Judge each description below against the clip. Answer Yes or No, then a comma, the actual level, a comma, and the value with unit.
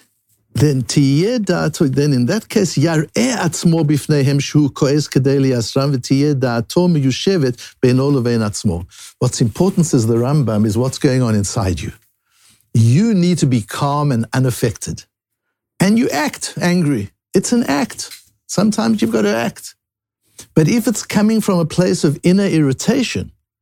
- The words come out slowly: Yes, slow, 115 wpm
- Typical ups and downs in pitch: No, wide, 6.3 semitones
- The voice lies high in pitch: No, medium, 145 Hz